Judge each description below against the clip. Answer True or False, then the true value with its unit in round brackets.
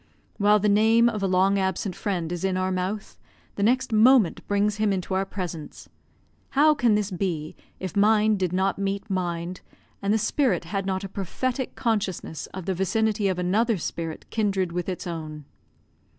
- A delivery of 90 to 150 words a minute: False (180 wpm)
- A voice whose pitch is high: True (195 Hz)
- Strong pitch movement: False (2.7 semitones)